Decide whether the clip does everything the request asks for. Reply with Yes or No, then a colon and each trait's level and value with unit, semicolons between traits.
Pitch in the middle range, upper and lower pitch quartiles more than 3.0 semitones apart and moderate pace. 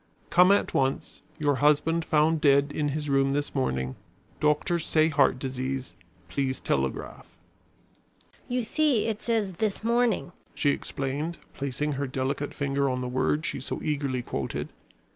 Yes: medium, 145 Hz; average, 3.4 semitones; average, 145 wpm